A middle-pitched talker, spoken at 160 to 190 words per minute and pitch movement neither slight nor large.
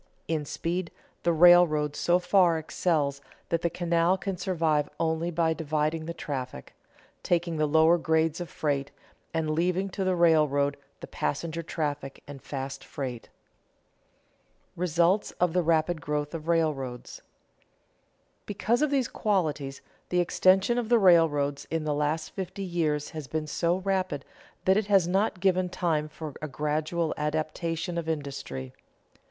No: medium, 165 Hz; average, 145 wpm; average, 3.0 semitones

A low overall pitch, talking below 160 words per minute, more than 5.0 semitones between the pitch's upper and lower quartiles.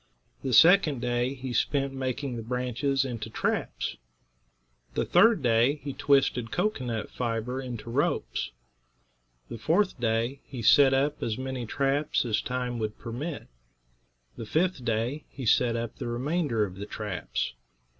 No: low, 125 Hz; average, 145 wpm; average, 3.2 semitones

